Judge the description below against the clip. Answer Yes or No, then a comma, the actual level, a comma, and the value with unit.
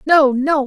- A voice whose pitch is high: Yes, very high, 280 Hz